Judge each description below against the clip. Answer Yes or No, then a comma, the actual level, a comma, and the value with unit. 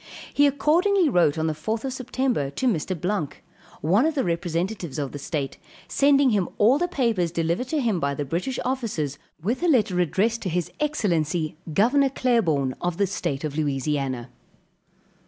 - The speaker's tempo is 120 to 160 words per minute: No, average, 170 wpm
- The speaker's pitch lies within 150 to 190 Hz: Yes, medium, 185 Hz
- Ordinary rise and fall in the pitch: No, wide, 8.7 semitones